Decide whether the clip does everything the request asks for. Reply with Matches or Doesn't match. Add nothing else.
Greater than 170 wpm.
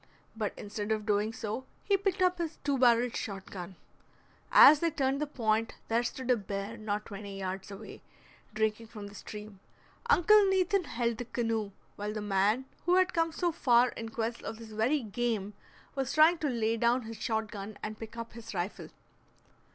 Matches